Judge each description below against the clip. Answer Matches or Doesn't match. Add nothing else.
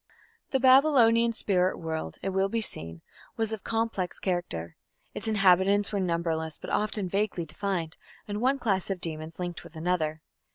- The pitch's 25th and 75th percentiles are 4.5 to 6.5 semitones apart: Matches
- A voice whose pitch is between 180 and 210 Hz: Matches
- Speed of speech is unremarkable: Matches